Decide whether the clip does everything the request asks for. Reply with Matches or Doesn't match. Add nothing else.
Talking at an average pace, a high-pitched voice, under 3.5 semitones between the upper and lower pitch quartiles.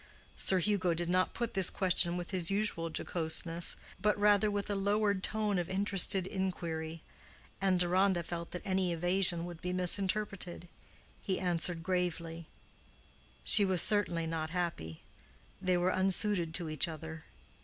Doesn't match